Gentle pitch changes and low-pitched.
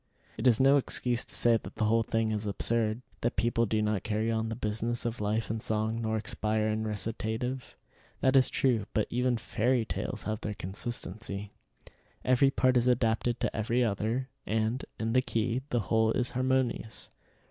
Yes: narrow, 2.2 semitones; low, 115 Hz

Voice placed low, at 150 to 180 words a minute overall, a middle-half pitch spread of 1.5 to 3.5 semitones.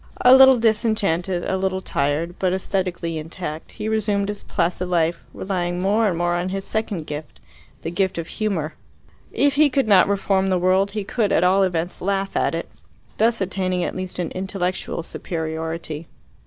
No: medium, 185 Hz; average, 175 wpm; average, 2.8 semitones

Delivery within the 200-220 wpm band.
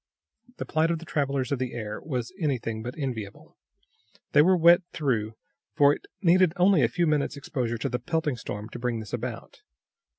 No: average, 190 wpm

